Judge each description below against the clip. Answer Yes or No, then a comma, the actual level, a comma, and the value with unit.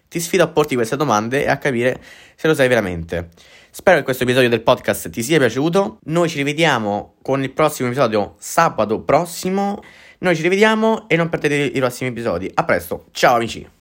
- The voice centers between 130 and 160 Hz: Yes, medium, 140 Hz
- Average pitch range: No, wide, 6.2 semitones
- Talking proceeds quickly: Yes, fast, 190 wpm